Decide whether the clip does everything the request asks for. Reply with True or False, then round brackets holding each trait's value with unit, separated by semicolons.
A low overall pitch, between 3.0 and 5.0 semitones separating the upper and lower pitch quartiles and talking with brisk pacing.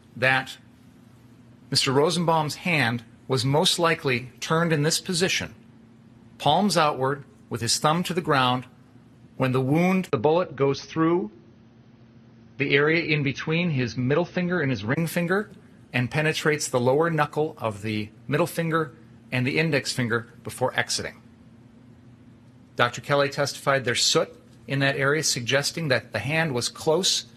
False (130 Hz; 4.6 semitones; 145 wpm)